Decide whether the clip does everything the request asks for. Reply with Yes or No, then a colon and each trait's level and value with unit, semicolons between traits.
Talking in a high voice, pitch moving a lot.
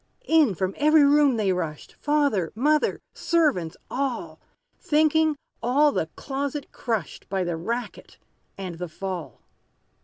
Yes: high, 245 Hz; wide, 8.2 semitones